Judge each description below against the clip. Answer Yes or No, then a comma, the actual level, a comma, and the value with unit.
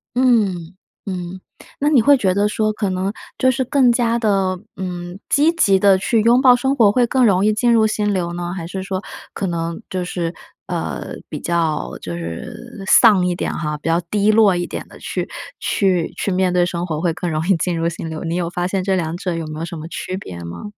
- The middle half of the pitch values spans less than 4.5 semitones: Yes, average, 4.0 semitones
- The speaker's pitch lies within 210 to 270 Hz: No, medium, 185 Hz